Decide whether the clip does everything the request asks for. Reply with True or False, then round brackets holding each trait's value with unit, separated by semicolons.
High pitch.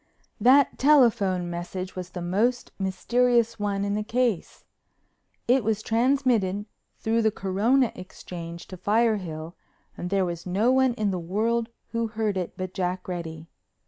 True (205 Hz)